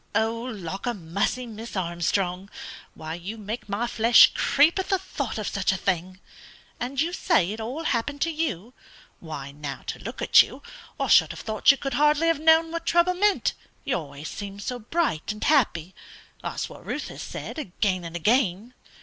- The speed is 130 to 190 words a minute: Yes, average, 185 wpm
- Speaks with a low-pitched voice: No, high, 220 Hz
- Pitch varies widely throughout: Yes, wide, 7.7 semitones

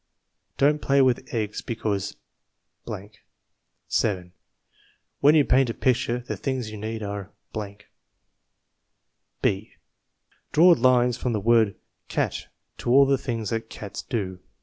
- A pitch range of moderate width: Yes, average, 3.7 semitones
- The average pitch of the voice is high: No, low, 115 Hz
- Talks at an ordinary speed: No, slow, 125 wpm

